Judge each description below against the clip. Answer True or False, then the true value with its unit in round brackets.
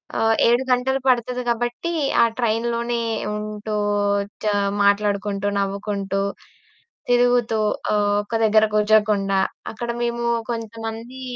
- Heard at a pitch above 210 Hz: True (225 Hz)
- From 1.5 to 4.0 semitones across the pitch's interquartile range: True (2.4 semitones)